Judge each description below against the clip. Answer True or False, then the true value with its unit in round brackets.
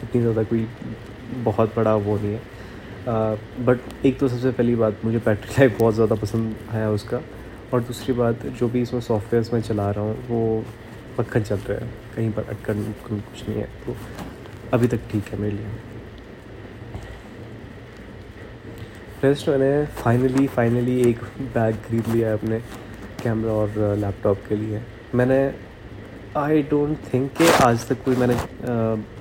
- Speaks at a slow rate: False (160 wpm)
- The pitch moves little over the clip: True (2.3 semitones)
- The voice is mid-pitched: False (115 Hz)